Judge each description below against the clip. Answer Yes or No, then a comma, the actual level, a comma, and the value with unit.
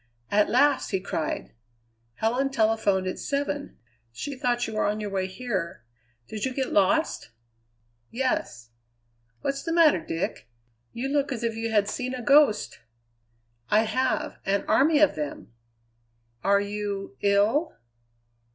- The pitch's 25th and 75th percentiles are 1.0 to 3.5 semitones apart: No, average, 5.2 semitones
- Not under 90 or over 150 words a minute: Yes, average, 140 wpm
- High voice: Yes, high, 225 Hz